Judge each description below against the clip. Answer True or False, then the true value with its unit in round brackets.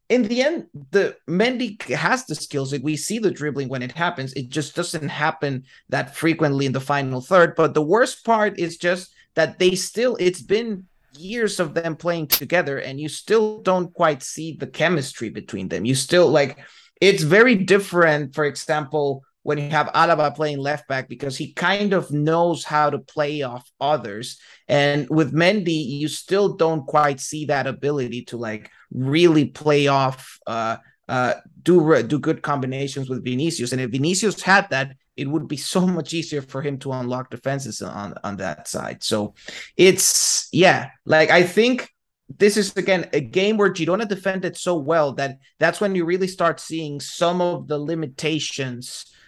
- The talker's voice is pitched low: False (155 Hz)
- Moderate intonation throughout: True (4.3 semitones)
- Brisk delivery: False (180 wpm)